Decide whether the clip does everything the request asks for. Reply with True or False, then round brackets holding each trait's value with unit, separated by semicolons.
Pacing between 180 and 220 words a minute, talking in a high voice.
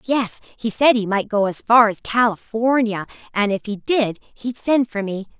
True (200 wpm; 225 Hz)